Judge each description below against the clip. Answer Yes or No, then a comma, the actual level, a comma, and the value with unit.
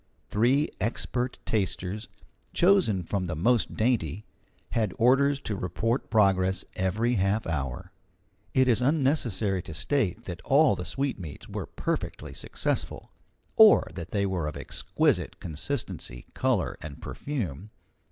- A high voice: No, low, 105 Hz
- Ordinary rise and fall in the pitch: No, wide, 5.7 semitones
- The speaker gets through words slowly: Yes, slow, 125 wpm